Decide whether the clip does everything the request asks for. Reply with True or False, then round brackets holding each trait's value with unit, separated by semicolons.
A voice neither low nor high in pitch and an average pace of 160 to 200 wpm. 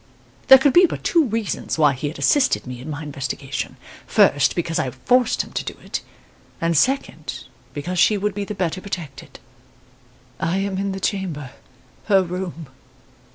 True (180 Hz; 170 wpm)